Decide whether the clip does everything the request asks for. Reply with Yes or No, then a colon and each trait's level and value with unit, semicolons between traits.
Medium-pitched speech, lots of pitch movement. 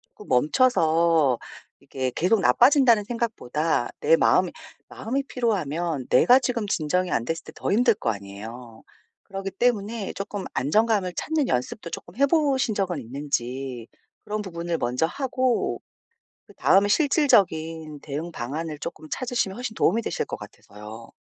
Yes: medium, 180 Hz; wide, 8.3 semitones